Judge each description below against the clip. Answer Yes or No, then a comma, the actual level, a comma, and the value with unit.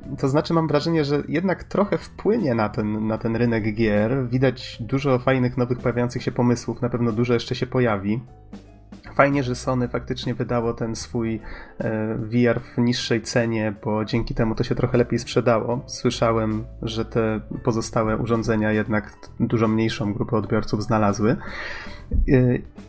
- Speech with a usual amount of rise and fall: No, narrow, 2.2 semitones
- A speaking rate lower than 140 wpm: No, average, 150 wpm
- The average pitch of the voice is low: Yes, low, 115 Hz